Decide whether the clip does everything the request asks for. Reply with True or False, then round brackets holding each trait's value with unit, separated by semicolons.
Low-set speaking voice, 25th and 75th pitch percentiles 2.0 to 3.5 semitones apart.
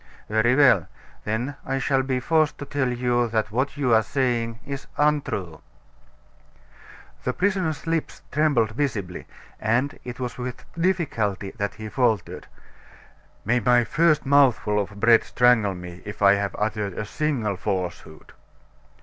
False (120 Hz; 4.9 semitones)